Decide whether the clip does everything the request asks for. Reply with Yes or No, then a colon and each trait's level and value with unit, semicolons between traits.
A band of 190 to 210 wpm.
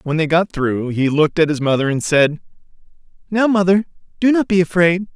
Yes: average, 200 wpm